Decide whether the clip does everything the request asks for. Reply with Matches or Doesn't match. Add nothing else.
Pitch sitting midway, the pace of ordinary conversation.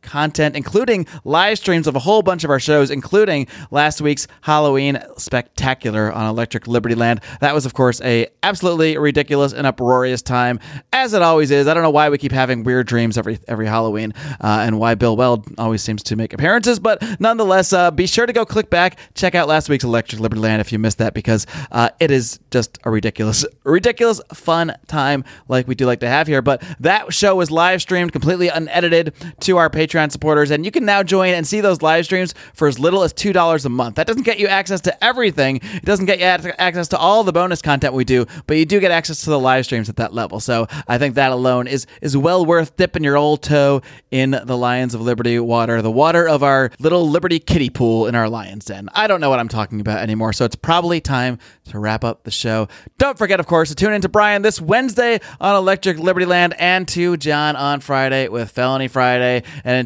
Doesn't match